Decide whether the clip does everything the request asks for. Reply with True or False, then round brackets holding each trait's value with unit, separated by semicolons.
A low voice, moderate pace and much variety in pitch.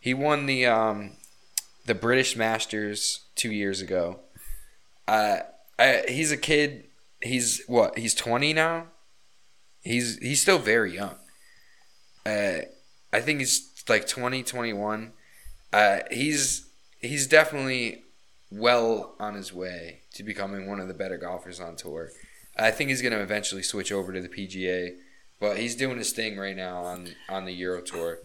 True (115 Hz; 155 wpm; 5.8 semitones)